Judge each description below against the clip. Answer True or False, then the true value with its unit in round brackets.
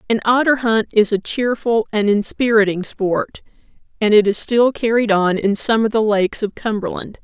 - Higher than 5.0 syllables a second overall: False (4.9 syllables/s)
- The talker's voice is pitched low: False (215 Hz)